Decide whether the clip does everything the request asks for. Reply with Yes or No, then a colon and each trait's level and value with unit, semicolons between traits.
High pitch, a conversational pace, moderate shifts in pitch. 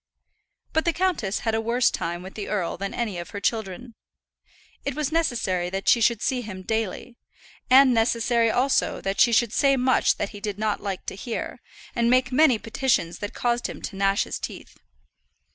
Yes: high, 225 Hz; average, 195 wpm; average, 4.1 semitones